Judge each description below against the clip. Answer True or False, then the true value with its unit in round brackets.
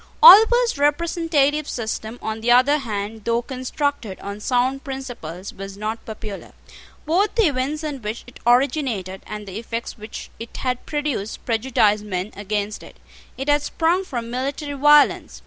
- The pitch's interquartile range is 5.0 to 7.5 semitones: True (5.4 semitones)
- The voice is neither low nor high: False (245 Hz)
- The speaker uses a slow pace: False (150 wpm)